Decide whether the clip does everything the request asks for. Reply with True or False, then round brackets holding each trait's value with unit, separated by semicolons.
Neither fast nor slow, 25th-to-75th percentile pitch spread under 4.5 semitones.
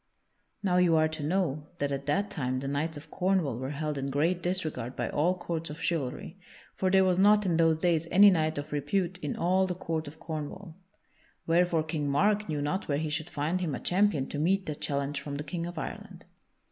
False (220 wpm; 3.8 semitones)